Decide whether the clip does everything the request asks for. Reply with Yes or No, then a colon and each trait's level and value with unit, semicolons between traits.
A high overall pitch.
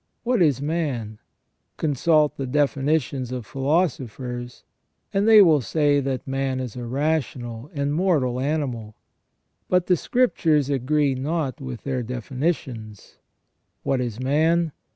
No: medium, 140 Hz